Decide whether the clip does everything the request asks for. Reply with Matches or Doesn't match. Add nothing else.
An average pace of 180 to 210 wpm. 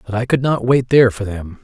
Doesn't match